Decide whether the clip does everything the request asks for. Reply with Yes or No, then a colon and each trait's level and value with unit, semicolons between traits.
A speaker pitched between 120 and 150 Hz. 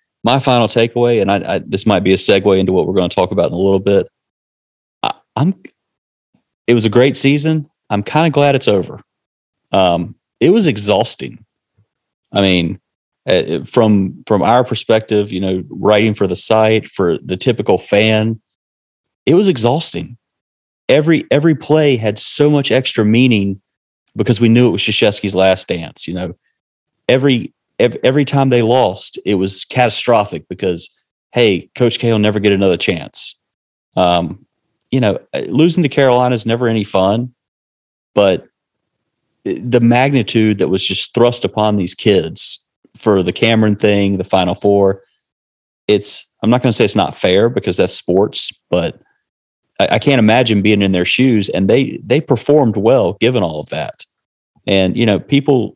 No: low, 110 Hz